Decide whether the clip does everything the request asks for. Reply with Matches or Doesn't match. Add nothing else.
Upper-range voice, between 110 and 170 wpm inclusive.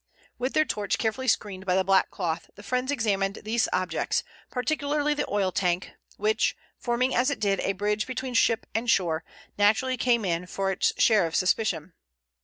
Doesn't match